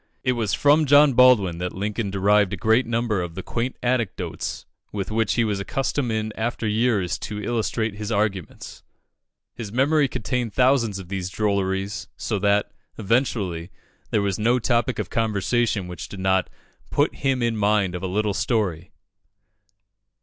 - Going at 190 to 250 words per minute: No, average, 160 wpm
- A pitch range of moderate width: Yes, average, 3.6 semitones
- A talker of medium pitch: No, low, 105 Hz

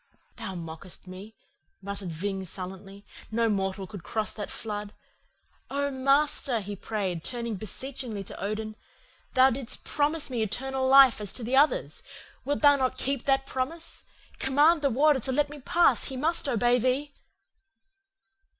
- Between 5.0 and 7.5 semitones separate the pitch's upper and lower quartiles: Yes, average, 5.3 semitones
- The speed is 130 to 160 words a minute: Yes, average, 155 wpm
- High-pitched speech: Yes, high, 245 Hz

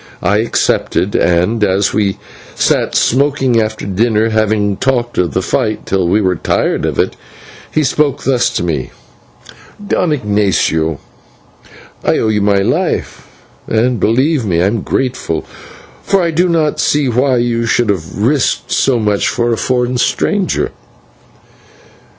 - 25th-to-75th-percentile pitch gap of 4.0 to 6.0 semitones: Yes, average, 4.4 semitones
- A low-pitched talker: Yes, low, 110 Hz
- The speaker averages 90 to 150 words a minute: Yes, average, 145 wpm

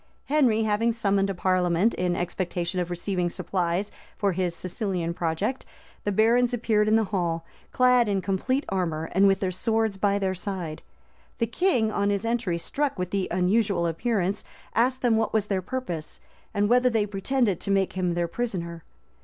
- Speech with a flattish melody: No, average, 3.9 semitones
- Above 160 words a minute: Yes, average, 175 wpm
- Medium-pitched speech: No, high, 195 Hz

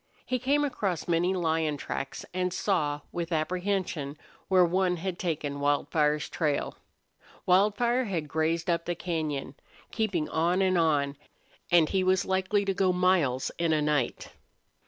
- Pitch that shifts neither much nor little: Yes, average, 3.6 semitones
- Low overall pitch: No, medium, 175 Hz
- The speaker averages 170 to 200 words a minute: No, average, 145 wpm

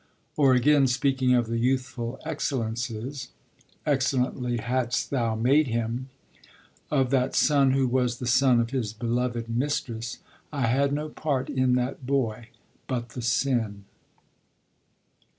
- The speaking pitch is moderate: No, low, 125 Hz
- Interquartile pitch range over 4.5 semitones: No, narrow, 2.4 semitones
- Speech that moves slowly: Yes, slow, 130 wpm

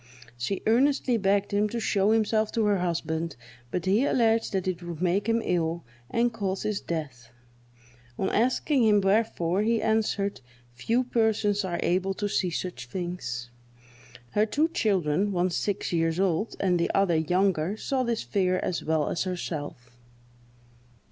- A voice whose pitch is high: Yes, high, 195 Hz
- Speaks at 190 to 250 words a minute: No, average, 155 wpm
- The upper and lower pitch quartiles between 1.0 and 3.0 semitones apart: No, average, 4.1 semitones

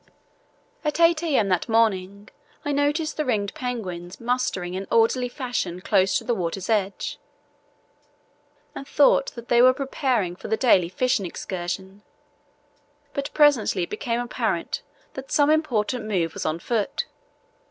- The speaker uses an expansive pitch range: Yes, wide, 5.7 semitones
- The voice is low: No, high, 225 Hz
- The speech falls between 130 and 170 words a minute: Yes, average, 140 wpm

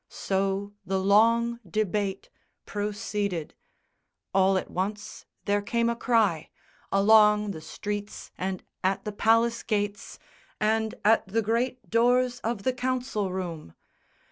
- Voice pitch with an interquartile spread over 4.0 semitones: No, average, 2.9 semitones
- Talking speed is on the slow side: Yes, slow, 120 wpm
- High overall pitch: Yes, high, 210 Hz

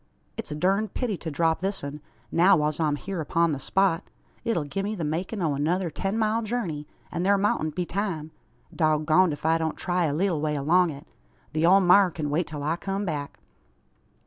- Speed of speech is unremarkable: No, fast, 210 wpm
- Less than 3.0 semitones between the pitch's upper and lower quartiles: No, average, 4.1 semitones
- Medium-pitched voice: Yes, medium, 170 Hz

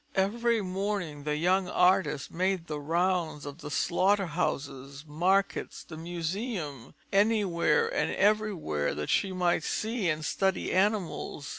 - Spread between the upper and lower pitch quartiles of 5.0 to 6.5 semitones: No, average, 4.4 semitones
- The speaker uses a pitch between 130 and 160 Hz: No, medium, 180 Hz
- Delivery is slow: Yes, slow, 125 wpm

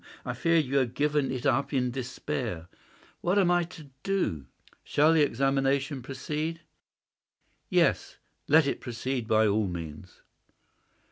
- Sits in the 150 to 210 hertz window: No, low, 135 Hz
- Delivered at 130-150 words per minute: Yes, average, 140 wpm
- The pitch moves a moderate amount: Yes, average, 4.1 semitones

